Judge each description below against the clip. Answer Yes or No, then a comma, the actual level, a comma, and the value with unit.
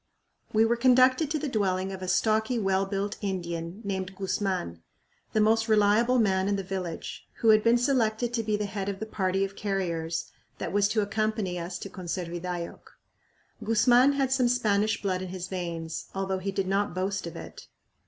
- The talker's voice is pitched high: Yes, high, 200 Hz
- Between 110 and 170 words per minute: No, average, 185 wpm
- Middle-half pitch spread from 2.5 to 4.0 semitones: Yes, average, 2.9 semitones